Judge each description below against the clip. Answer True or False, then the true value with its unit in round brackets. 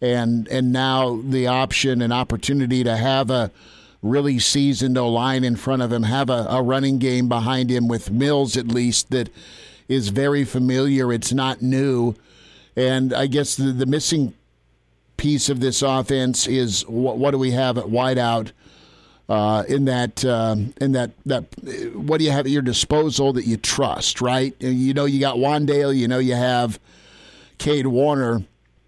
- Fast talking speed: False (170 wpm)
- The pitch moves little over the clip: True (2.2 semitones)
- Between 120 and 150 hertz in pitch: True (130 Hz)